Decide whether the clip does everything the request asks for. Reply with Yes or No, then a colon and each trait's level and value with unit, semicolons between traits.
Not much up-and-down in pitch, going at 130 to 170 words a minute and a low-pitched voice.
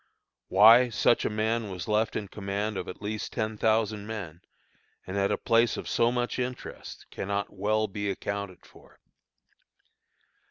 Yes: narrow, 1.9 semitones; average, 155 wpm; low, 105 Hz